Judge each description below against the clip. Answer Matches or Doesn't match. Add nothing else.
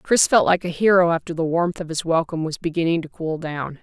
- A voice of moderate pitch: Matches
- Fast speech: Matches